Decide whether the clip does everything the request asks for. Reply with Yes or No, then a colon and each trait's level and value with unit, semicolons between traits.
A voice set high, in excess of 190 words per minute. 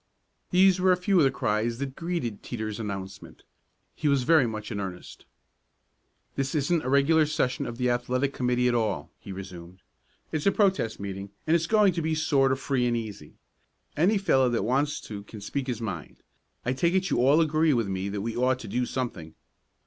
No: low, 125 Hz; average, 200 wpm